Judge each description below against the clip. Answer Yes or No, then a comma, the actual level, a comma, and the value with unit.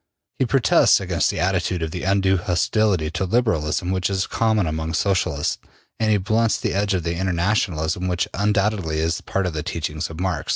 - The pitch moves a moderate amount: Yes, average, 3.8 semitones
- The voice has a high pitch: No, very low, 95 Hz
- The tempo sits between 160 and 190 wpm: Yes, average, 180 wpm